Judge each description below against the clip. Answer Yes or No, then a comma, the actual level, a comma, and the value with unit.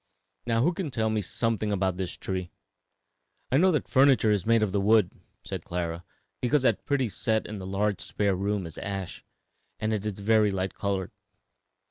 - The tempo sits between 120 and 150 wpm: No, average, 185 wpm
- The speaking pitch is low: Yes, low, 105 Hz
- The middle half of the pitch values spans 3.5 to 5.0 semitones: No, average, 3.1 semitones